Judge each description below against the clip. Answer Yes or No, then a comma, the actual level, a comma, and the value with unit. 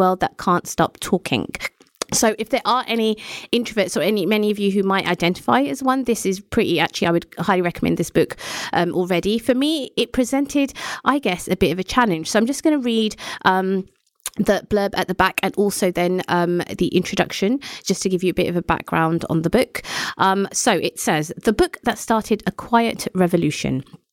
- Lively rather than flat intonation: No, average, 4.5 semitones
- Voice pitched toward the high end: Yes, high, 200 Hz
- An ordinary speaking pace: No, fast, 210 wpm